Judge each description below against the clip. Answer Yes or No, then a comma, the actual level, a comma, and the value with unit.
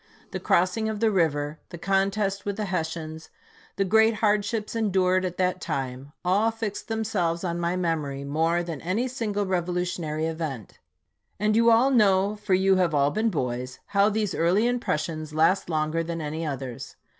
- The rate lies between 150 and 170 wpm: Yes, average, 165 wpm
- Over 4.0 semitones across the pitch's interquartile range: Yes, average, 4.6 semitones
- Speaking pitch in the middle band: Yes, medium, 180 Hz